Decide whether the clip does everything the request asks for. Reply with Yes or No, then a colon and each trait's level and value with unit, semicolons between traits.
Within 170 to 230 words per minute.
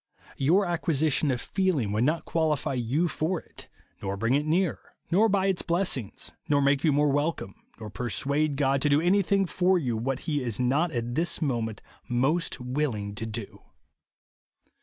Yes: average, 180 wpm